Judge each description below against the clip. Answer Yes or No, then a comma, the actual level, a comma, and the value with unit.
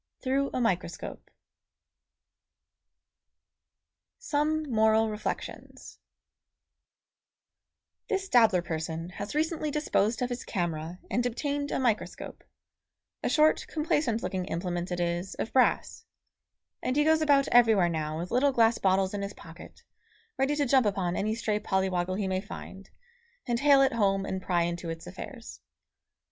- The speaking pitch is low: No, high, 215 Hz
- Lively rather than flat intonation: Yes, wide, 6.7 semitones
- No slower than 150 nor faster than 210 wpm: No, average, 140 wpm